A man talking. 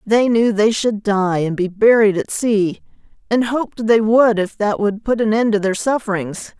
No: female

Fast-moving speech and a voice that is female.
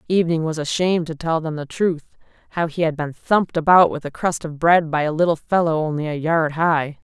Yes: fast, 220 wpm; female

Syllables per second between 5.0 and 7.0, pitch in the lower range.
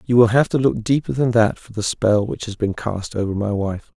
Yes: 5.2 syllables/s; low, 110 Hz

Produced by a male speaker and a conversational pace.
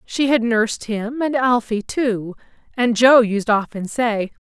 No: female; average, 160 wpm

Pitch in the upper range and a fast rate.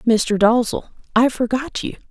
No: high, 235 Hz; average, 145 wpm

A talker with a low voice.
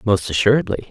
Yes: low, 100 Hz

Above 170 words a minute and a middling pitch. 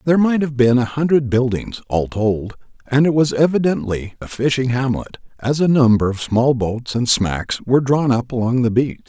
No: average, 200 wpm; low, 125 Hz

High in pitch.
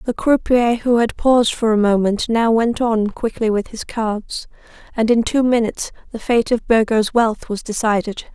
Yes: high, 225 Hz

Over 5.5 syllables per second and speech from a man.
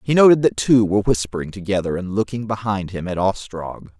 Yes: 5.7 syllables/s; male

